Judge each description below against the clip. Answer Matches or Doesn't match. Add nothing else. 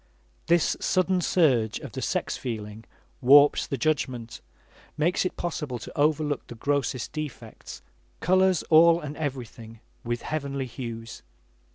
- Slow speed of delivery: Matches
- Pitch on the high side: Doesn't match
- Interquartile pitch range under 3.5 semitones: Doesn't match